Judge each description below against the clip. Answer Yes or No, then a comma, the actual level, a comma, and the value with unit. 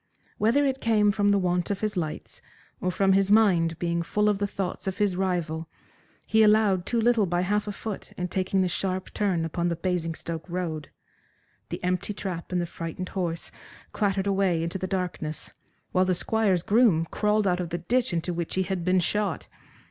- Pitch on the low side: No, medium, 185 Hz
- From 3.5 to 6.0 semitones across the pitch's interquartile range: No, average, 3.0 semitones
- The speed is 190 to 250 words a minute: Yes, average, 195 wpm